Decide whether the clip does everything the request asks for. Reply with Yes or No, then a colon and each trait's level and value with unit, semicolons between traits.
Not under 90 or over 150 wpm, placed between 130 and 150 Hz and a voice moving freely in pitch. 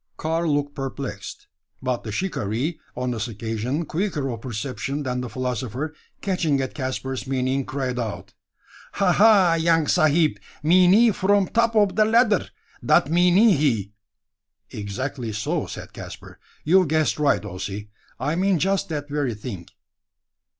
Yes: average, 140 wpm; medium, 140 Hz; wide, 5.8 semitones